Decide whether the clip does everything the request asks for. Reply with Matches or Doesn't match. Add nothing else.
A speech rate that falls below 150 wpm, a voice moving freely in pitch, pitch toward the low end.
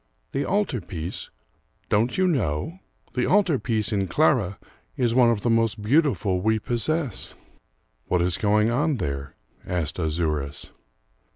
Matches